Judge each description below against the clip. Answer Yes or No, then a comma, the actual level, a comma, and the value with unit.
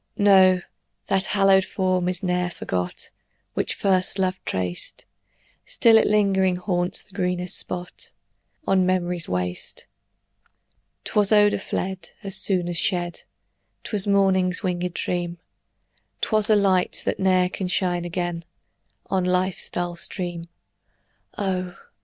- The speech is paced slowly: Yes, slow, 125 wpm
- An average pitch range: No, narrow, 1.5 semitones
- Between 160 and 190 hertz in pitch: Yes, medium, 185 Hz